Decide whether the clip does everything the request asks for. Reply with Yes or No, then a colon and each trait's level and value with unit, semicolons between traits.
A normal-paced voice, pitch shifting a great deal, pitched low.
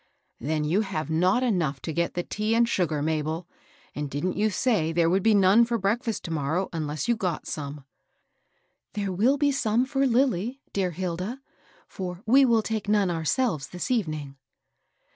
No: average, 180 wpm; wide, 6.2 semitones; medium, 185 Hz